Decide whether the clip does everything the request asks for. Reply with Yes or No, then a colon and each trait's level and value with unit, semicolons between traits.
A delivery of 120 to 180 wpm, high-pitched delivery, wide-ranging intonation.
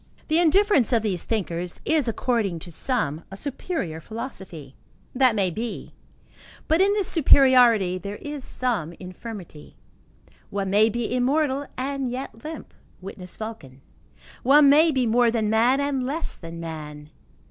Yes: average, 145 wpm; high, 230 Hz; wide, 6.9 semitones